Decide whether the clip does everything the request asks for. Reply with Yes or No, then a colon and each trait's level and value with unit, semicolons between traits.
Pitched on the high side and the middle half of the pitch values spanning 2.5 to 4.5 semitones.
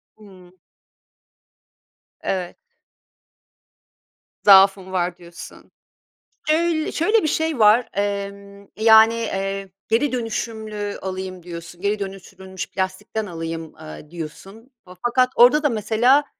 Yes: high, 200 Hz; average, 3.5 semitones